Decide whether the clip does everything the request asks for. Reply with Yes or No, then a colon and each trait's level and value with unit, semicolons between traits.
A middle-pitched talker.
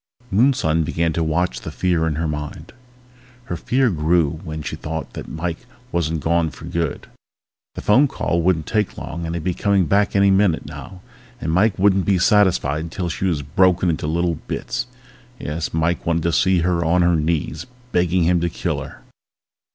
No: very low, 85 Hz